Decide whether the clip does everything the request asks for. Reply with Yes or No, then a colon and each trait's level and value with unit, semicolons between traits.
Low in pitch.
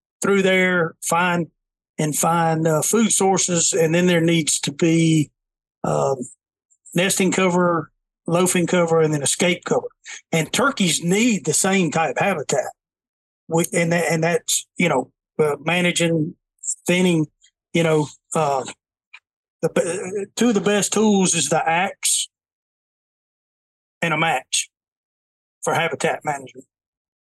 No: medium, 170 Hz